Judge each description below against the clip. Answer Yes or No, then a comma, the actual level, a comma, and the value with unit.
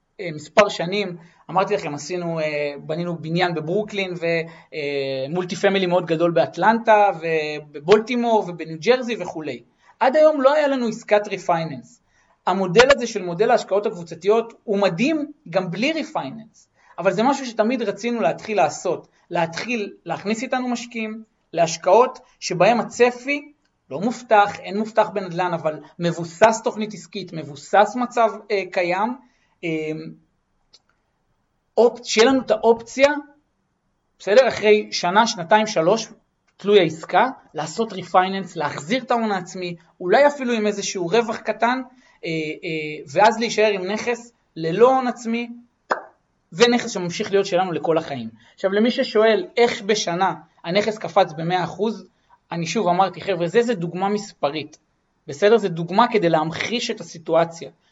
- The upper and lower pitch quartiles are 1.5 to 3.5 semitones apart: No, average, 5.2 semitones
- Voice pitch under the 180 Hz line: No, high, 205 Hz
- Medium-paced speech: Yes, average, 125 wpm